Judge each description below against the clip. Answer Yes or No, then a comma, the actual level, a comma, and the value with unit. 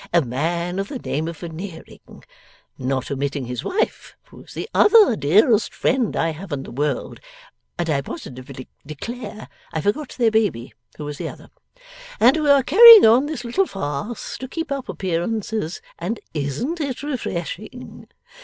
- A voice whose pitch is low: No, high, 195 Hz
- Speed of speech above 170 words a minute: No, average, 165 wpm